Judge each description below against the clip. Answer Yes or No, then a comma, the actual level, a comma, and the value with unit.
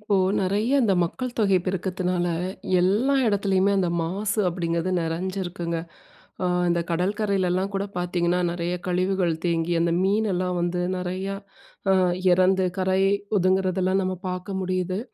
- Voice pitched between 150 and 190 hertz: Yes, medium, 185 Hz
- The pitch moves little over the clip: Yes, narrow, 1.7 semitones